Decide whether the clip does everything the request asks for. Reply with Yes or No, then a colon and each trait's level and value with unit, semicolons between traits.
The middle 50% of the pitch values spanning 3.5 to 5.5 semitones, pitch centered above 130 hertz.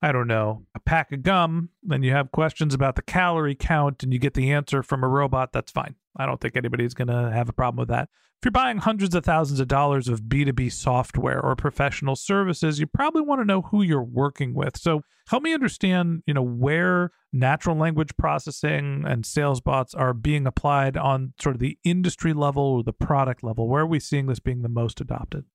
Yes: average, 3.9 semitones; medium, 140 Hz